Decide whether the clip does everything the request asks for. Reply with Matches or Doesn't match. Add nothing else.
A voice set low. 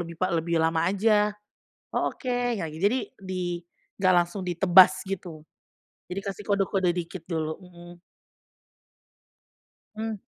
Doesn't match